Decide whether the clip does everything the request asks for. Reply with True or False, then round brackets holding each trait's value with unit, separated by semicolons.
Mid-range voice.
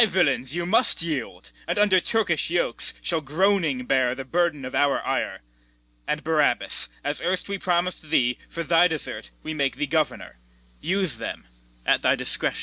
True (160 Hz)